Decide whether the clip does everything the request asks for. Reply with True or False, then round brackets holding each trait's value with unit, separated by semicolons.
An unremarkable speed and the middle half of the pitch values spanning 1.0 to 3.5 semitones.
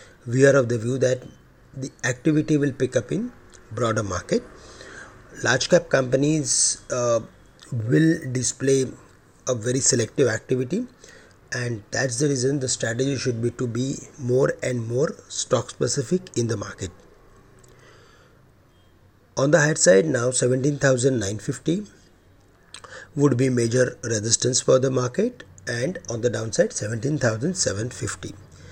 False (125 wpm; 3.0 semitones)